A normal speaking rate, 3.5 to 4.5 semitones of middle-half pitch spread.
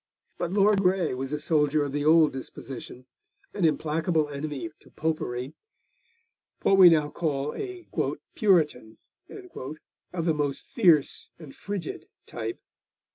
No: slow, 130 wpm; average, 3.8 semitones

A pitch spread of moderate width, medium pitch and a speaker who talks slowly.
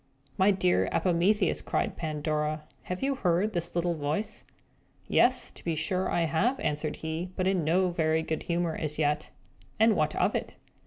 No: average, 3.2 semitones; medium, 170 Hz; average, 170 wpm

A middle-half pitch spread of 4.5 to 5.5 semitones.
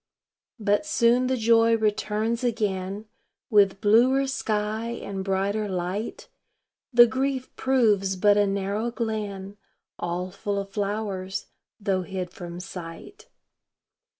No: average, 3.1 semitones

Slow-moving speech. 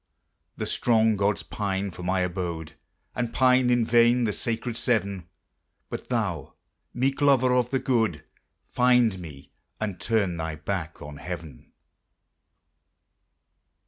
Yes: slow, 125 wpm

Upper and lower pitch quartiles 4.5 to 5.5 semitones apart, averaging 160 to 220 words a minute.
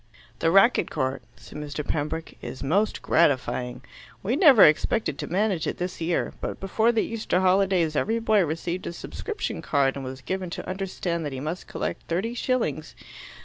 Yes: average, 5.1 semitones; average, 175 wpm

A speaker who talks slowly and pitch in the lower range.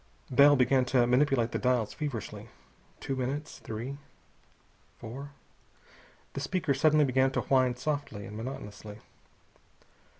Yes: slow, 120 wpm; low, 130 Hz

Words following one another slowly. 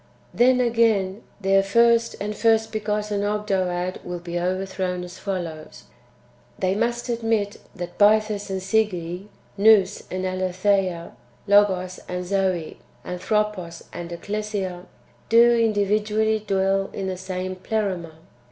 Yes: slow, 120 wpm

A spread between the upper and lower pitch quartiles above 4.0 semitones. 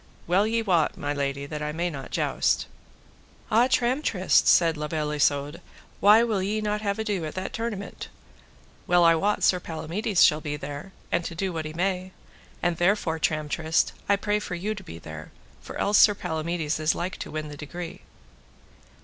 Yes: average, 4.8 semitones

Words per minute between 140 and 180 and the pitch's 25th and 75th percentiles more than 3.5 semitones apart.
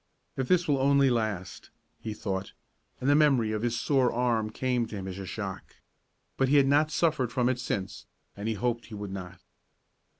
No: average, 200 wpm; average, 4.6 semitones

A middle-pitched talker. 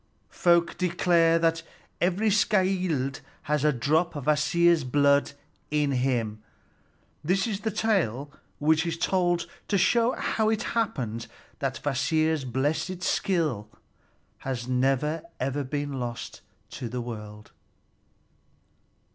Yes: medium, 150 Hz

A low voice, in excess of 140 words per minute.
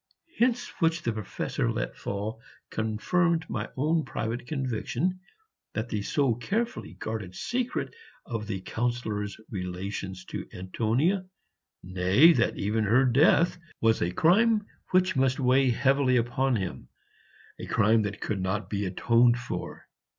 No: low, 120 Hz; slow, 135 wpm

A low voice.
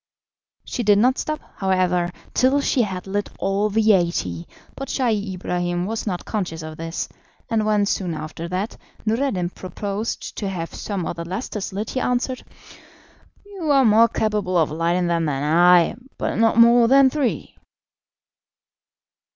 No: high, 200 Hz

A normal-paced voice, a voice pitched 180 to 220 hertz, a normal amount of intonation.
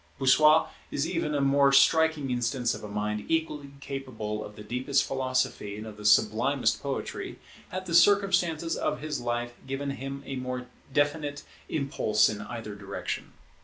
No: average, 160 wpm; low, 135 Hz; average, 4.7 semitones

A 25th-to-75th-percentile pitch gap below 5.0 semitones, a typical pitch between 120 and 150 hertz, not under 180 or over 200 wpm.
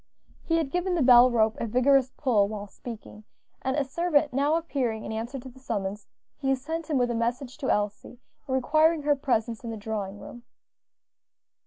No: average, 4.5 semitones; very high, 255 Hz; average, 185 wpm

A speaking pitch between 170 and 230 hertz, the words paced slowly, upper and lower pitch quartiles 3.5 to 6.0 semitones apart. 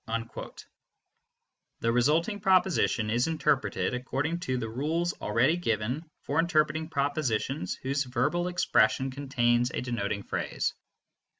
No: medium, 140 Hz; slow, 115 wpm; average, 5.0 semitones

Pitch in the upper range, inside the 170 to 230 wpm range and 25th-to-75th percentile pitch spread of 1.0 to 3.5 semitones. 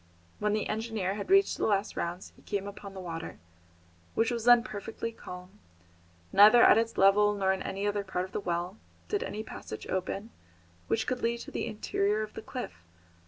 Yes: high, 205 Hz; average, 195 wpm; average, 2.8 semitones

